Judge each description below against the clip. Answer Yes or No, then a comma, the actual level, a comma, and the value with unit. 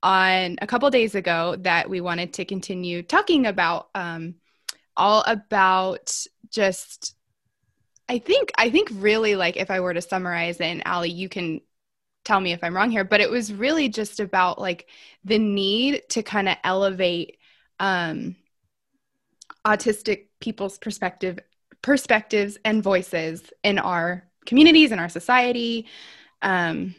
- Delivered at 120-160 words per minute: Yes, average, 145 wpm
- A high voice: Yes, high, 195 Hz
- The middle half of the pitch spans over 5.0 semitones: No, average, 3.6 semitones